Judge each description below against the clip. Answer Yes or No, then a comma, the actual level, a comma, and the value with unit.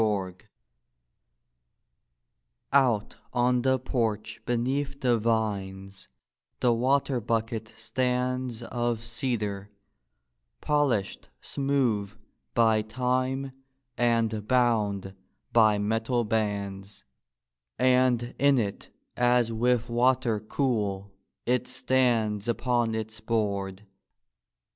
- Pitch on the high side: No, low, 115 Hz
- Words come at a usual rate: No, slow, 90 wpm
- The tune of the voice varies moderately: Yes, average, 3.0 semitones